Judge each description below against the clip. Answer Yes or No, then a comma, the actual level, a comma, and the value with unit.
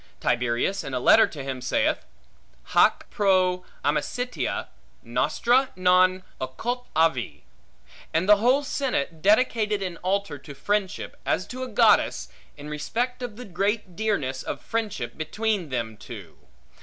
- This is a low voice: No, medium, 185 Hz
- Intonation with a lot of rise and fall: Yes, wide, 7.2 semitones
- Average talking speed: No, slow, 130 wpm